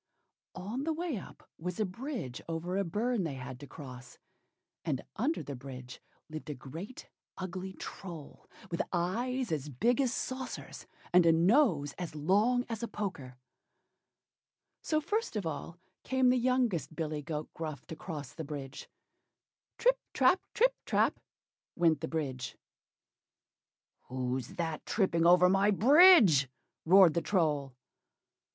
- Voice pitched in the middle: Yes, medium, 175 Hz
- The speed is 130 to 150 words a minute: Yes, average, 140 wpm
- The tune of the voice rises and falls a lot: Yes, wide, 8.0 semitones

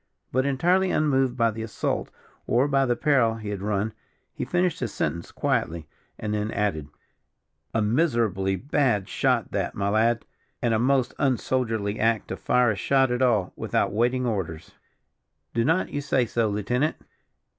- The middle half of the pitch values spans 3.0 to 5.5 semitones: Yes, average, 4.1 semitones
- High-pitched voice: No, low, 115 Hz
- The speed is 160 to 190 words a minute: Yes, average, 165 wpm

